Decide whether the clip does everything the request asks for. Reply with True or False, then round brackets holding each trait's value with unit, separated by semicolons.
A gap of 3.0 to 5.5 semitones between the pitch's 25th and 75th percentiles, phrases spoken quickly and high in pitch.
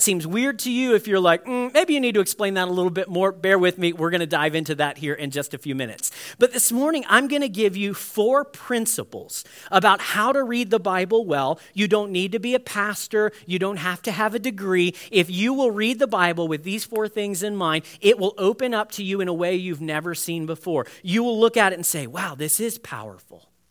True (4.9 semitones; 255 wpm; 195 Hz)